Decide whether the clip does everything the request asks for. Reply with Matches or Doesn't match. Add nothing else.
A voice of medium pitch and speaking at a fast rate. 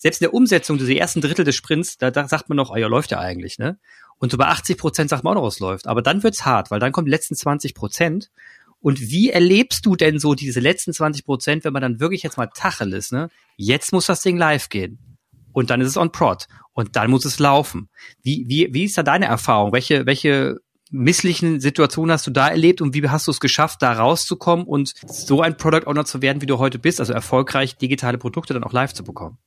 Matches